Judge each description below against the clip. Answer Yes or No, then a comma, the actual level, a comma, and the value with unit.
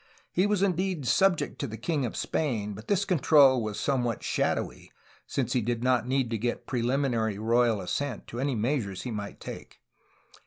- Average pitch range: Yes, average, 4.2 semitones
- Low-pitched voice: Yes, low, 125 Hz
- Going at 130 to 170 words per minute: No, average, 185 wpm